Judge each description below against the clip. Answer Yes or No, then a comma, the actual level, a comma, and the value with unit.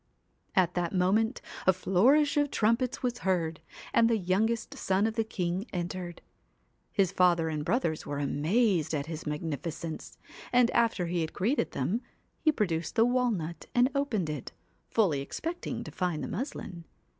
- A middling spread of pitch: No, wide, 5.8 semitones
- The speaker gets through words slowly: No, average, 160 wpm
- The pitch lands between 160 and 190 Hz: Yes, medium, 185 Hz